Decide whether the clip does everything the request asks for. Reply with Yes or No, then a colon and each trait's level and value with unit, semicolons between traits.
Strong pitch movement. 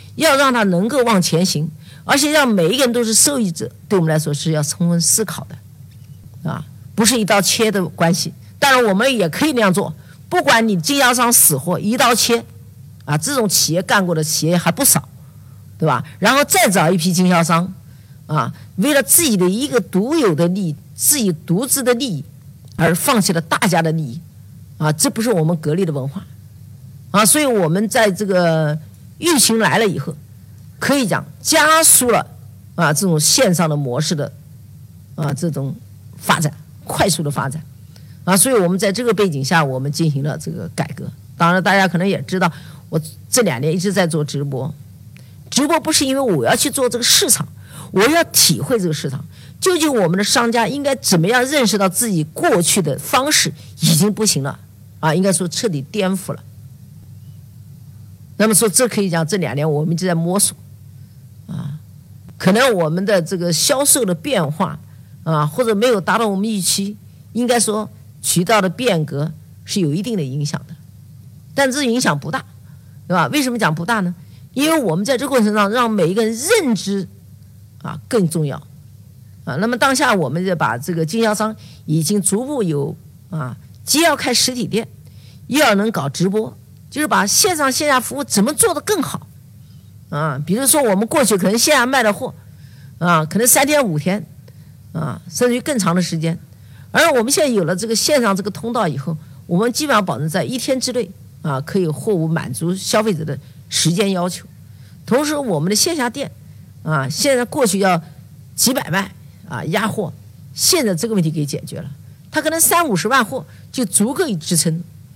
Yes: wide, 7.6 semitones